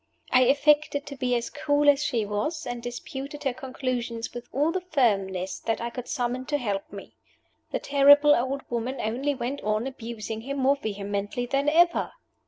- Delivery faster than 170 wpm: Yes, average, 185 wpm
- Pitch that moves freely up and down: No, average, 3.7 semitones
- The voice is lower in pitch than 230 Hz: No, very high, 255 Hz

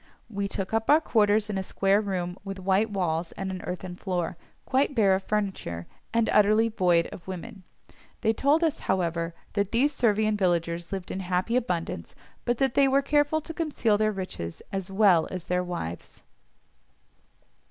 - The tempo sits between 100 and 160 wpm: No, average, 175 wpm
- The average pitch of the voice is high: Yes, high, 195 Hz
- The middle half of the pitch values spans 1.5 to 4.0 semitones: Yes, average, 3.7 semitones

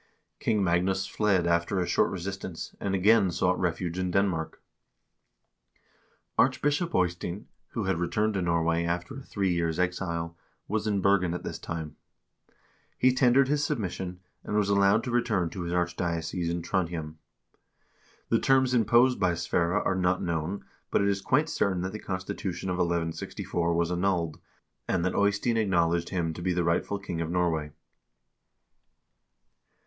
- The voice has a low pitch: Yes, very low, 90 Hz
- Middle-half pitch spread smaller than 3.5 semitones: Yes, average, 2.9 semitones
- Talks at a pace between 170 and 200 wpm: No, average, 155 wpm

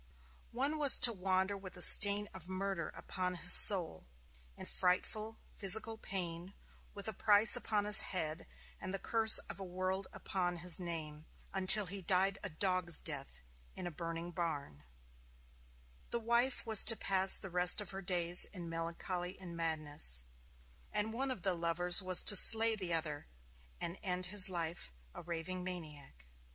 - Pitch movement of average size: Yes, average, 3.0 semitones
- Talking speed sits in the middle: Yes, average, 165 wpm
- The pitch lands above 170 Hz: Yes, medium, 185 Hz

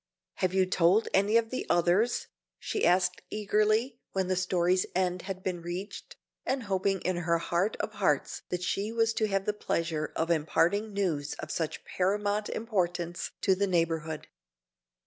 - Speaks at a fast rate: No, average, 165 wpm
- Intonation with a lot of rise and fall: No, average, 3.2 semitones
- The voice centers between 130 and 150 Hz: No, medium, 185 Hz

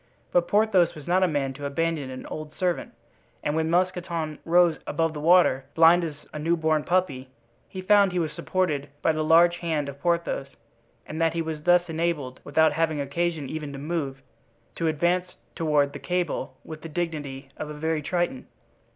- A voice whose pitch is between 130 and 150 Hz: No, medium, 160 Hz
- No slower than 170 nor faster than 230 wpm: Yes, average, 185 wpm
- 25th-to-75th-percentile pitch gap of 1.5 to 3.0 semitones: Yes, average, 2.7 semitones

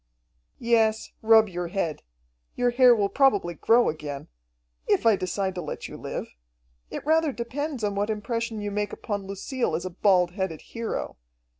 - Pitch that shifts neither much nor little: Yes, average, 4.1 semitones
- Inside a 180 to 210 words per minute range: No, average, 165 wpm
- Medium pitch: No, high, 210 Hz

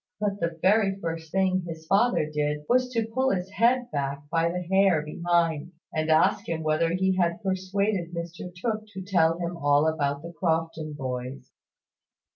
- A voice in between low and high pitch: Yes, medium, 170 Hz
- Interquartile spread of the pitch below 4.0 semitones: Yes, average, 3.5 semitones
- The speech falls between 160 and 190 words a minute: Yes, average, 170 wpm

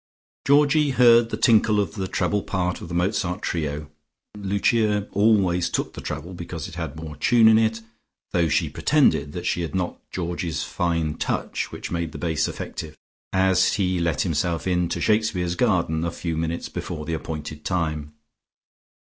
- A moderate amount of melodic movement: Yes, average, 4.0 semitones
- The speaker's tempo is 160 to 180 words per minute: Yes, average, 170 wpm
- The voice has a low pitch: Yes, very low, 90 Hz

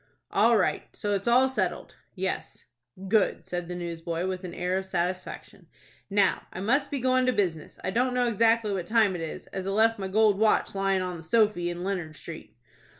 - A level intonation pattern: No, average, 4.0 semitones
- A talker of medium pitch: No, high, 195 Hz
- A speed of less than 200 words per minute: No, fast, 205 wpm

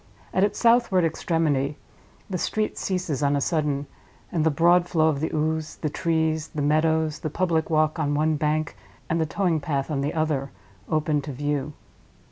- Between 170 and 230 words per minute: Yes, average, 180 wpm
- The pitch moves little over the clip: Yes, narrow, 1.9 semitones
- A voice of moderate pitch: Yes, medium, 155 Hz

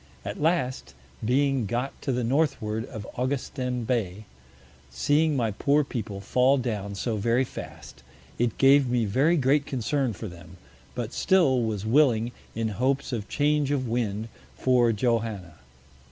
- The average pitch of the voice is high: No, low, 120 Hz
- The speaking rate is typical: Yes, average, 145 wpm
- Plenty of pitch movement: No, average, 4.0 semitones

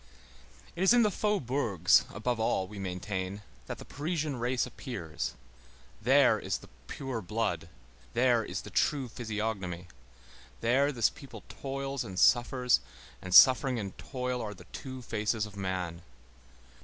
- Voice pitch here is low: Yes, low, 115 Hz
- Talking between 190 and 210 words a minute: No, average, 145 wpm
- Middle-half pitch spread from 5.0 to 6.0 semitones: Yes, wide, 5.4 semitones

